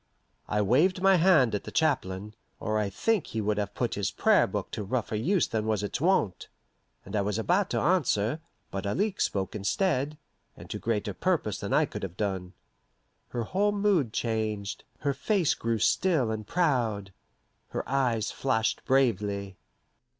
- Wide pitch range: Yes, wide, 7.8 semitones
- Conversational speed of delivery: Yes, average, 170 wpm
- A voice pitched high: No, low, 115 Hz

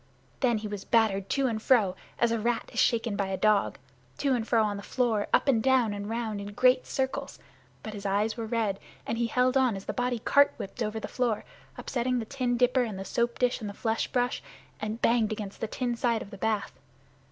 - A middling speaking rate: No, fast, 230 wpm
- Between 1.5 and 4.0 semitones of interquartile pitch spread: Yes, average, 2.8 semitones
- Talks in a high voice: Yes, high, 230 Hz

